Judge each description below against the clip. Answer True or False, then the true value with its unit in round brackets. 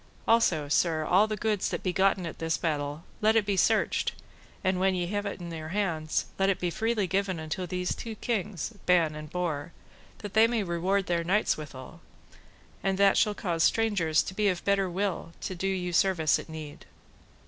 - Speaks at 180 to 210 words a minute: True (200 wpm)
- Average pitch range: True (3.5 semitones)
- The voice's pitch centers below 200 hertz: True (185 Hz)